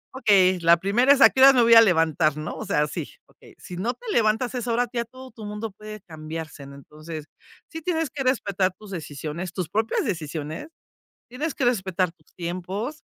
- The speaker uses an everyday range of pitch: No, wide, 6.9 semitones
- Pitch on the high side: Yes, high, 200 Hz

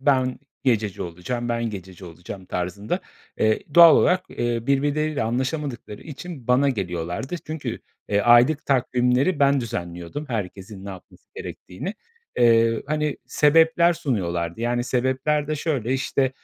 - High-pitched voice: No, low, 125 Hz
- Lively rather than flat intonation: Yes, wide, 5.7 semitones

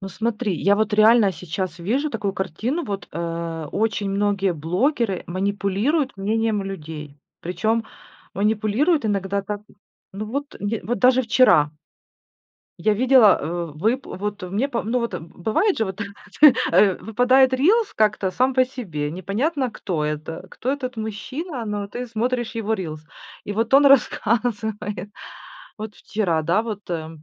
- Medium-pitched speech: No, high, 210 Hz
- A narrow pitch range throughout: No, average, 4.5 semitones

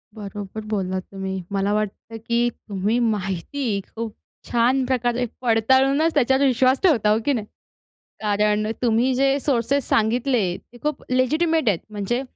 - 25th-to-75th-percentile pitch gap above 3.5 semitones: Yes, average, 4.0 semitones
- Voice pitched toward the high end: Yes, high, 235 Hz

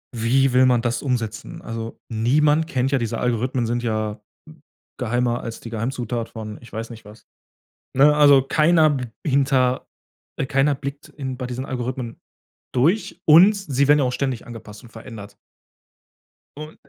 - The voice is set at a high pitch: No, low, 125 Hz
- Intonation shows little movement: No, average, 3.2 semitones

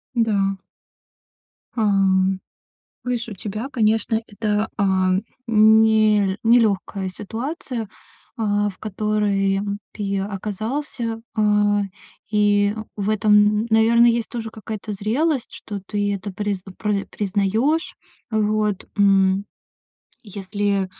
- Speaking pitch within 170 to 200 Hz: No, high, 210 Hz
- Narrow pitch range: Yes, narrow, 1.8 semitones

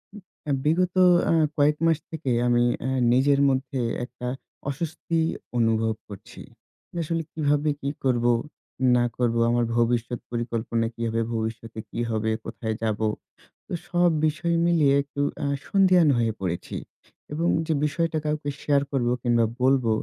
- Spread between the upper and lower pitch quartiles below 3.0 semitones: No, average, 4.8 semitones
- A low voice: Yes, low, 130 Hz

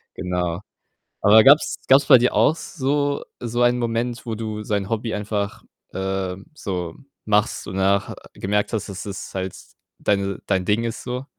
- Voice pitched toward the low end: Yes, low, 105 Hz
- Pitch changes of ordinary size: Yes, average, 3.8 semitones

